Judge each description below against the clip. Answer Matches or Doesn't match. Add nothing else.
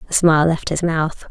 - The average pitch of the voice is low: Doesn't match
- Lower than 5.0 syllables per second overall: Doesn't match